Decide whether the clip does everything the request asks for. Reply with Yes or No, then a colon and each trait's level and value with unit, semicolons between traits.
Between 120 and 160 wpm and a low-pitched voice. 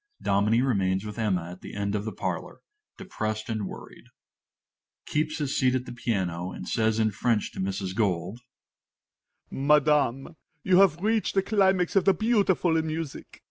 No: average, 175 wpm; low, 120 Hz